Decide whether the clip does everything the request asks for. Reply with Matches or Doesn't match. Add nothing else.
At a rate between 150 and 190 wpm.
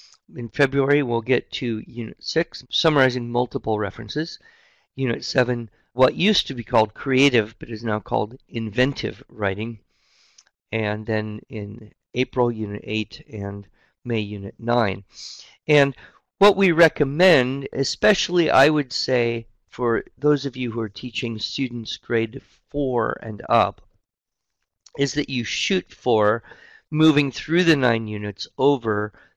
Doesn't match